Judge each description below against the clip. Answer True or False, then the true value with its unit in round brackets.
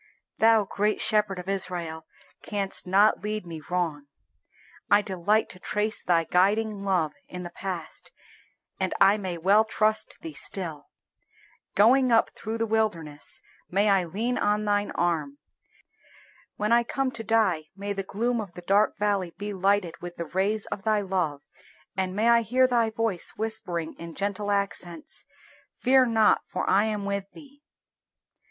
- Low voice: False (200 Hz)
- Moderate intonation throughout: True (3.3 semitones)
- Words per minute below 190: True (160 wpm)